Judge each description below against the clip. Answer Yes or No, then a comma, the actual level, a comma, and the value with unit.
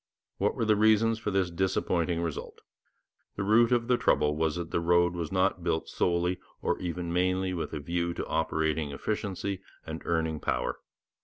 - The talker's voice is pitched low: Yes, very low, 90 Hz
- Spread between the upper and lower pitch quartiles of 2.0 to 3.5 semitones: Yes, average, 3.0 semitones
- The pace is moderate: Yes, average, 175 wpm